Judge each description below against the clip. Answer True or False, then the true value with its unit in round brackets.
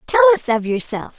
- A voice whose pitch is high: True (240 Hz)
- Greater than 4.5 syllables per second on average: True (5.8 syllables/s)